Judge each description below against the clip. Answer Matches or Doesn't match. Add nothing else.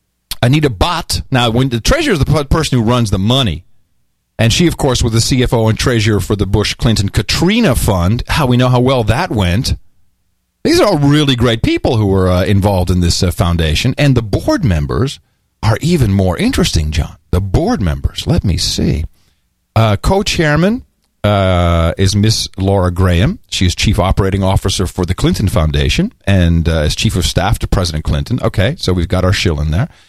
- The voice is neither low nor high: Doesn't match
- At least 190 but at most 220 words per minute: Matches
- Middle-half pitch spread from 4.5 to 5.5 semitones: Matches